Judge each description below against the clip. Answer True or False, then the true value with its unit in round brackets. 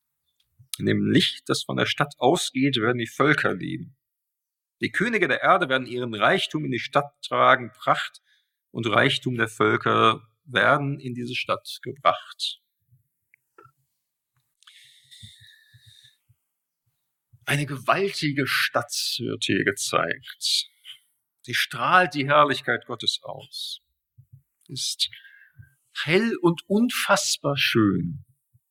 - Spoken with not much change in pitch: False (3.5 semitones)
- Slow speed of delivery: True (105 wpm)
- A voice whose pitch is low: True (130 Hz)